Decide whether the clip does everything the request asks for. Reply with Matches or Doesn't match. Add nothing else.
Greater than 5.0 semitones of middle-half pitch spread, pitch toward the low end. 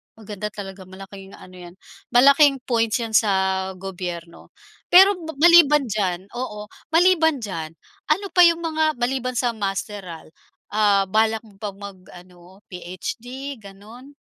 Doesn't match